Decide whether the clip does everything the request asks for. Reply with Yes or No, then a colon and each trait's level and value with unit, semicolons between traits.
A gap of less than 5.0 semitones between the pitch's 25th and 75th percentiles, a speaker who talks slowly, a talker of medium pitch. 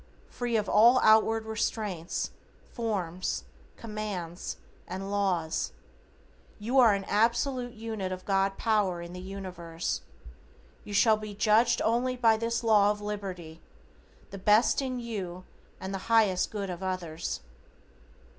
No: average, 3.4 semitones; slow, 130 wpm; high, 205 Hz